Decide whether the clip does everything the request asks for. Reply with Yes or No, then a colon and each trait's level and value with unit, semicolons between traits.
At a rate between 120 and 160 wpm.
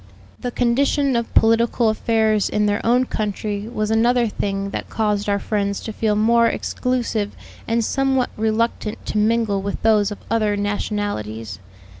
Yes: average, 150 wpm